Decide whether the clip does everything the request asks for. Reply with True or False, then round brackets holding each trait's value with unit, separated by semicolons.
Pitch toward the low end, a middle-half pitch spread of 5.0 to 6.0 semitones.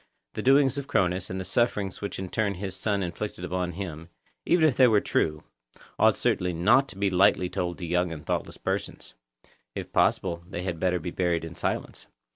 False (90 Hz; 2.8 semitones)